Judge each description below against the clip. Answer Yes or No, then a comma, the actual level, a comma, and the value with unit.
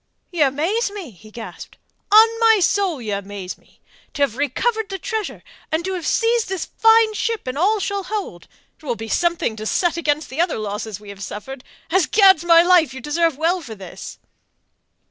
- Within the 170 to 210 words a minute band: Yes, average, 185 wpm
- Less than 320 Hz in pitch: No, very high, 330 Hz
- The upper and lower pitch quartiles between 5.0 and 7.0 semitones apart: No, wide, 8.6 semitones